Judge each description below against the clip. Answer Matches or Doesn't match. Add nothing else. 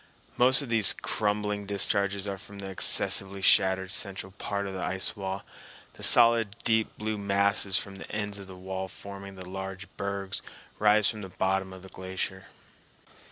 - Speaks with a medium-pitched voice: Doesn't match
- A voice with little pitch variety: Matches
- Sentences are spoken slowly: Doesn't match